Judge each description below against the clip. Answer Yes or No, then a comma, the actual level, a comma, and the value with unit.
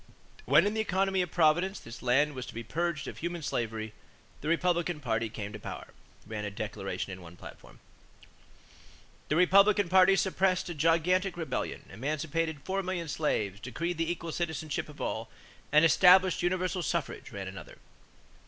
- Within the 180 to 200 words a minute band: No, average, 160 wpm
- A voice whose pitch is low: No, medium, 165 Hz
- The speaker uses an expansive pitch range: Yes, wide, 6.4 semitones